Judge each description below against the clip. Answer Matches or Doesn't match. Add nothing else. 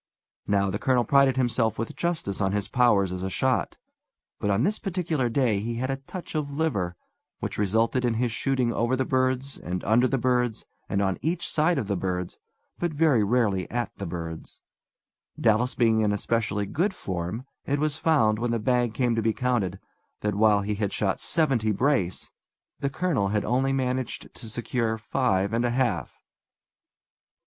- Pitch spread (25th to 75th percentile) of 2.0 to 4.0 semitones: Doesn't match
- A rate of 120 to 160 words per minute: Doesn't match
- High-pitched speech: Doesn't match